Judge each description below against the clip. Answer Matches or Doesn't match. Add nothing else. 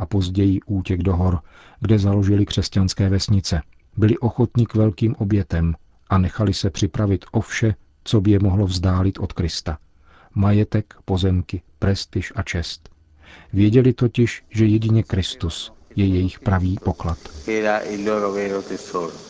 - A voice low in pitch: Matches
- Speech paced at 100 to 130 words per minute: Matches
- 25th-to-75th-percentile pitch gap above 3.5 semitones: Doesn't match